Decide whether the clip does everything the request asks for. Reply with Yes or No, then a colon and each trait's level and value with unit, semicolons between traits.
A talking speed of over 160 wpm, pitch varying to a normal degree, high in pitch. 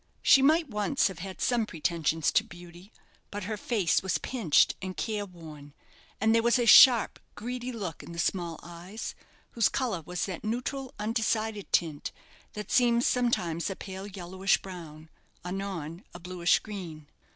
No: average, 155 wpm; average, 4.8 semitones; high, 195 Hz